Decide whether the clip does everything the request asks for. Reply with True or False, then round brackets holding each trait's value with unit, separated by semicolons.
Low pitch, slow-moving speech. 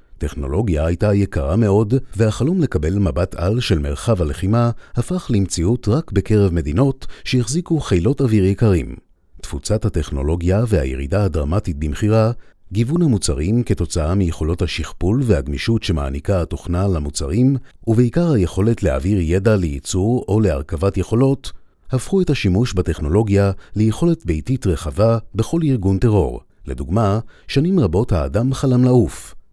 False (100 Hz; 115 wpm)